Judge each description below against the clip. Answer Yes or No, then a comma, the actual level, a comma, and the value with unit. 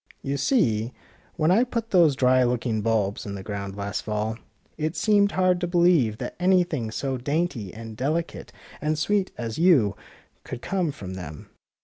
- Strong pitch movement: Yes, wide, 8.2 semitones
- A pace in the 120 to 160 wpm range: No, average, 170 wpm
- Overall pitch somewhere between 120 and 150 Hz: Yes, low, 135 Hz